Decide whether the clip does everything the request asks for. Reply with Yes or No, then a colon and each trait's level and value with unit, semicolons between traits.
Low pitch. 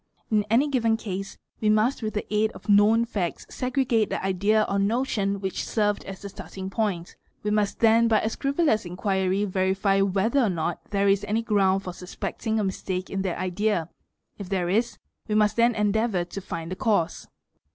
No: high, 205 Hz